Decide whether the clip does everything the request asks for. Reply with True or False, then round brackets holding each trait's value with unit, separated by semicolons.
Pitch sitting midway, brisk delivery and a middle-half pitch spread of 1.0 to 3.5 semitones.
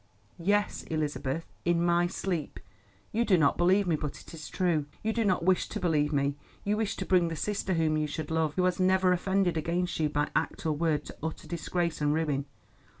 True (170 Hz; 210 wpm; 3.2 semitones)